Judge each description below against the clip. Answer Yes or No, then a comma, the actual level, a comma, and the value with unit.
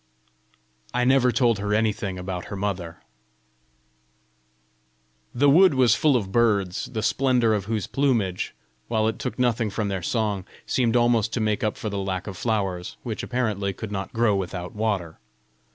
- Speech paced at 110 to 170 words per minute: Yes, average, 165 wpm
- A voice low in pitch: Yes, low, 110 Hz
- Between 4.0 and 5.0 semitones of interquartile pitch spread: No, average, 3.5 semitones